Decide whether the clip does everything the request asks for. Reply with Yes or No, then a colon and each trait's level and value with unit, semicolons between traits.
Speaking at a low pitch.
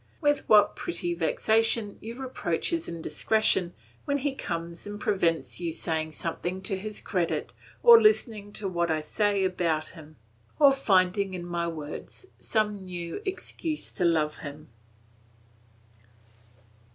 No: high, 190 Hz